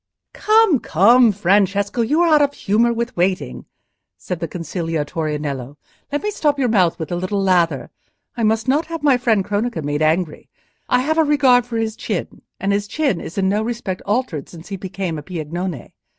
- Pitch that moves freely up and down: Yes, wide, 6.3 semitones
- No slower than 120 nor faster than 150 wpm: No, average, 195 wpm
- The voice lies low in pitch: No, high, 200 Hz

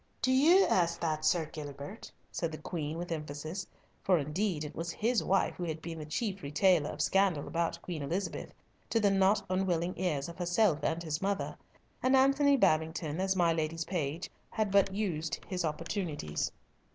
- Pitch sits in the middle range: Yes, medium, 170 Hz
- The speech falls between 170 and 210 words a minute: Yes, average, 175 wpm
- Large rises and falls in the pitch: No, average, 3.9 semitones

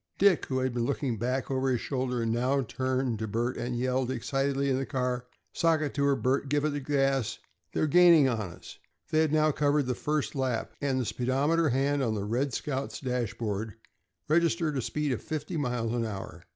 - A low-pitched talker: Yes, low, 130 Hz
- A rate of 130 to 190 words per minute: No, fast, 205 wpm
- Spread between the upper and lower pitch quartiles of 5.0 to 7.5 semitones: No, average, 2.9 semitones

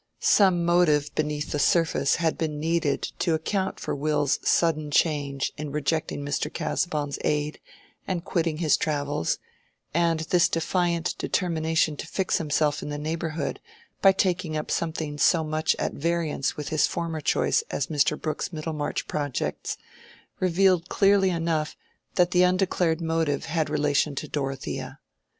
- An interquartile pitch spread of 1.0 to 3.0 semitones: Yes, narrow, 2.4 semitones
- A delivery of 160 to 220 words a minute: No, average, 150 wpm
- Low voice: No, medium, 160 Hz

